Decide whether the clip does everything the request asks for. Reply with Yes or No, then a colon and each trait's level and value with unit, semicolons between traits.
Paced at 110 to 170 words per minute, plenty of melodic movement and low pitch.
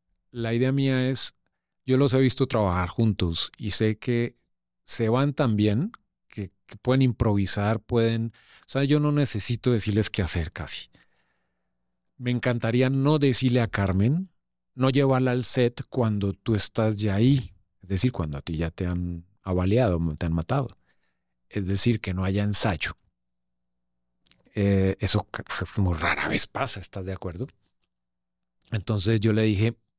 Yes: average, 155 wpm; wide, 5.7 semitones; low, 105 Hz